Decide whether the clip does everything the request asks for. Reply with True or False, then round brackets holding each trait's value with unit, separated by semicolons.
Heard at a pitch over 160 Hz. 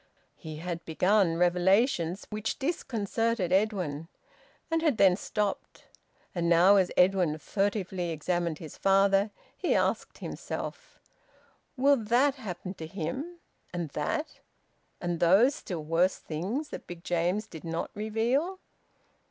True (190 Hz)